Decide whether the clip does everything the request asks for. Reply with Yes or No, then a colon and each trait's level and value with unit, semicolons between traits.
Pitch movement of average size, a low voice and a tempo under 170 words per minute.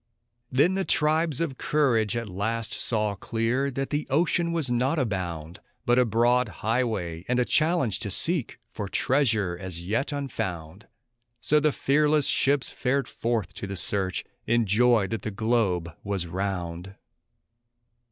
No: wide, 5.8 semitones; low, 115 Hz; average, 150 wpm